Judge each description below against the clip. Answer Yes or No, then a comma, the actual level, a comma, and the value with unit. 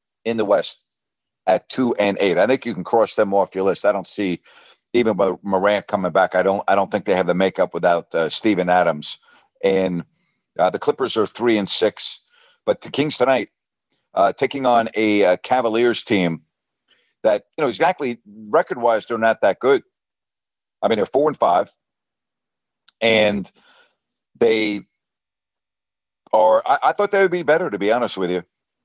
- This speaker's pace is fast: No, average, 180 wpm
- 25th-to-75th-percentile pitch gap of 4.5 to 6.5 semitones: Yes, wide, 5.5 semitones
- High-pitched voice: No, low, 110 Hz